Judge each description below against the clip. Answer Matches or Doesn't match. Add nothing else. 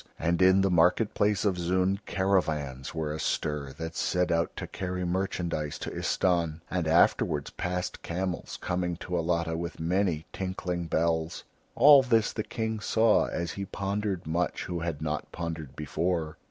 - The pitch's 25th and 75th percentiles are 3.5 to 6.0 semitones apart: Doesn't match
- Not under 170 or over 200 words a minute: Doesn't match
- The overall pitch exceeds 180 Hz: Doesn't match